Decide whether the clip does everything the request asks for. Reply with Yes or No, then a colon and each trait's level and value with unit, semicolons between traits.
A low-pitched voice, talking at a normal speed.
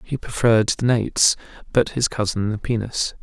Yes: low, 110 Hz; average, 170 wpm